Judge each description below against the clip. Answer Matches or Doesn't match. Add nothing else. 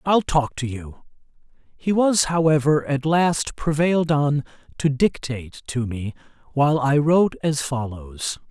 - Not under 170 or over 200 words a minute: Doesn't match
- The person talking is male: Matches